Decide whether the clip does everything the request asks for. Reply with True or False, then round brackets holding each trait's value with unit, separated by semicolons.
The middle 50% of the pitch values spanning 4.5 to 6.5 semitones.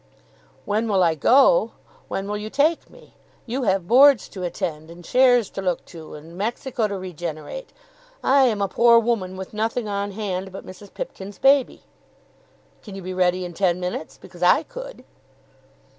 True (4.9 semitones)